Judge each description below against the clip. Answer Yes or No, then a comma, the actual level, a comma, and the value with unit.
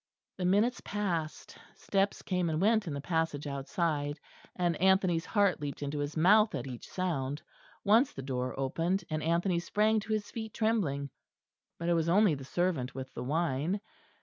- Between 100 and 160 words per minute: No, average, 175 wpm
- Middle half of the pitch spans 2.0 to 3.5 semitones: No, wide, 5.5 semitones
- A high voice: No, medium, 170 Hz